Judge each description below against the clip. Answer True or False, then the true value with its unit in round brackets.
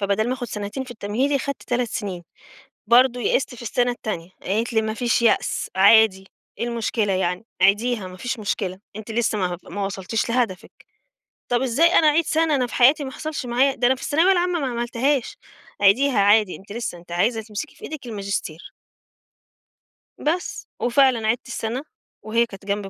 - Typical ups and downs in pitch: True (4.2 semitones)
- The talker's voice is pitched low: False (235 Hz)